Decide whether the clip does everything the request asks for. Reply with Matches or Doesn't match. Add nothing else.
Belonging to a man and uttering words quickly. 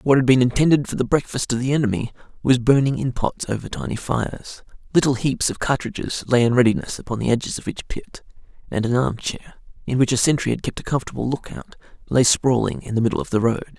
Matches